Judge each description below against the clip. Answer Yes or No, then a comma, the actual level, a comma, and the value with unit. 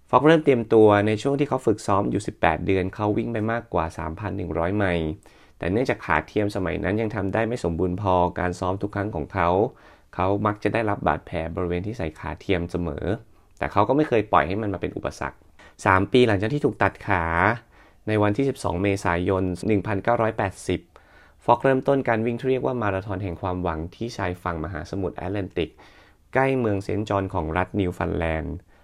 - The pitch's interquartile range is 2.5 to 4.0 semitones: Yes, average, 3.7 semitones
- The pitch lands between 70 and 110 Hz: Yes, low, 100 Hz